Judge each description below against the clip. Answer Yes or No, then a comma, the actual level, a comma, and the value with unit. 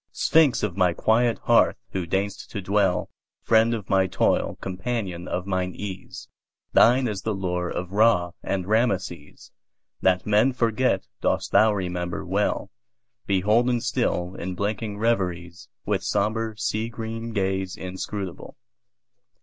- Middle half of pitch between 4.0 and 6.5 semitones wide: No, average, 3.6 semitones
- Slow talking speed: Yes, slow, 115 wpm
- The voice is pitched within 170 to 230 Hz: No, low, 100 Hz